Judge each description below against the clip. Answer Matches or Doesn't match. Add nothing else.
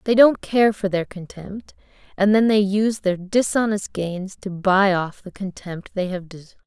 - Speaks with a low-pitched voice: Doesn't match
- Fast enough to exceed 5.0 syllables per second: Doesn't match